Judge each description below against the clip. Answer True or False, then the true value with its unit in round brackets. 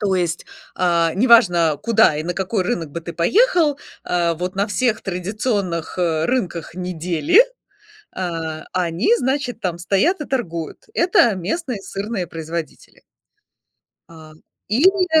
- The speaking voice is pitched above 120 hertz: True (185 Hz)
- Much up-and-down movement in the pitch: True (6.2 semitones)